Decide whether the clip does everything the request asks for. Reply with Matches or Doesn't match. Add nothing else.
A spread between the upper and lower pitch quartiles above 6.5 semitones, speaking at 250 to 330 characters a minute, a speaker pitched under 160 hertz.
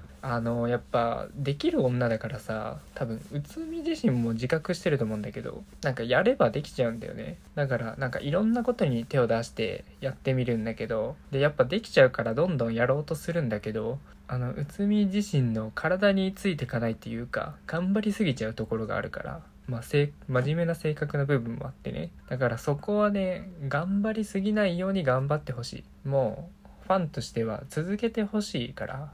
Doesn't match